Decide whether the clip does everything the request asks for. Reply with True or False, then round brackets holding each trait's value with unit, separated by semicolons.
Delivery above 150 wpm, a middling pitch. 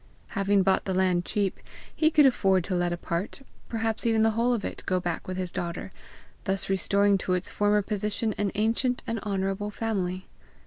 False (190 wpm; 200 Hz)